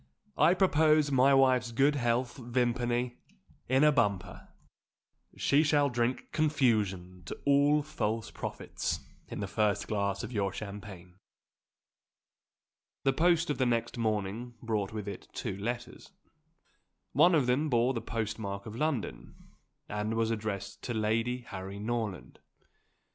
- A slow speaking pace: Yes, slow, 130 wpm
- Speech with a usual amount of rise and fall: Yes, average, 4.4 semitones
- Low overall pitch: Yes, low, 120 Hz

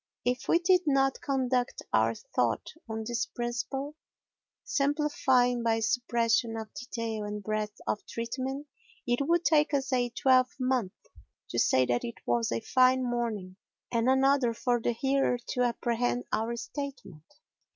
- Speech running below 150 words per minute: Yes, slow, 135 wpm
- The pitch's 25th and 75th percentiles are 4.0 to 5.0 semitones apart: No, average, 3.1 semitones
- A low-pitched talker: No, high, 245 Hz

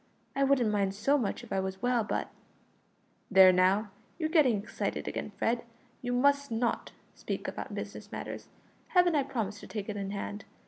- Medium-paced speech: Yes, average, 185 wpm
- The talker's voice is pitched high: Yes, high, 225 Hz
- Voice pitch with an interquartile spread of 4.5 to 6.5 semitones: Yes, wide, 5.4 semitones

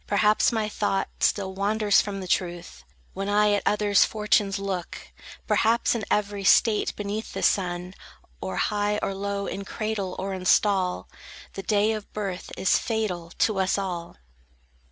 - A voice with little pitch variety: Yes, narrow, 1.8 semitones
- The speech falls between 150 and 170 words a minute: Yes, average, 155 wpm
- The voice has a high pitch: Yes, high, 200 Hz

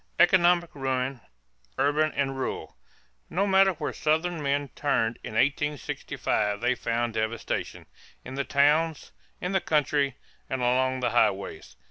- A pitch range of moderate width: Yes, average, 3.8 semitones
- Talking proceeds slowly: Yes, slow, 130 wpm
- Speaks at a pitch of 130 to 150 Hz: Yes, medium, 140 Hz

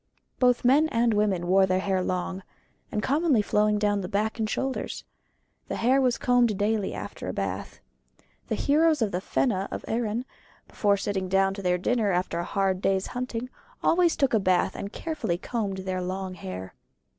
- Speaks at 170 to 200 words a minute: Yes, average, 185 wpm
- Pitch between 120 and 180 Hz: No, high, 205 Hz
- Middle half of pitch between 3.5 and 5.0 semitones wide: Yes, average, 4.4 semitones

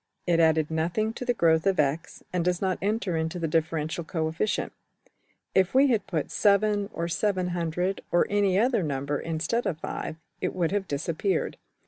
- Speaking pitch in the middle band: Yes, medium, 175 Hz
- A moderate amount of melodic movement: Yes, average, 3.8 semitones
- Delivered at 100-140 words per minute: No, average, 150 wpm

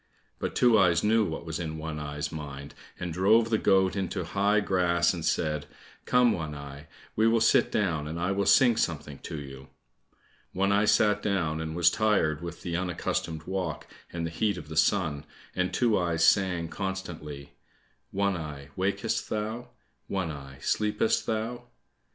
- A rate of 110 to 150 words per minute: No, average, 170 wpm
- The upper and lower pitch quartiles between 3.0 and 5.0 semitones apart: Yes, average, 4.5 semitones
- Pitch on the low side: Yes, very low, 90 Hz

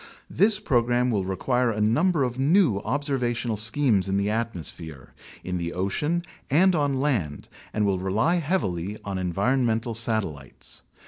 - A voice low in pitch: Yes, low, 115 Hz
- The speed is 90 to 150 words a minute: Yes, average, 145 wpm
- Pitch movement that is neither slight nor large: No, wide, 6.2 semitones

